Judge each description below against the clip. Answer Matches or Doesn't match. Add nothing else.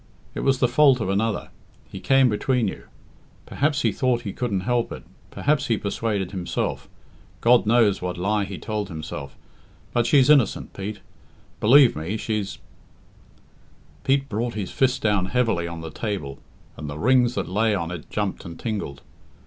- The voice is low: Matches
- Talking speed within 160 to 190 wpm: Matches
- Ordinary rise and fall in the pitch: Matches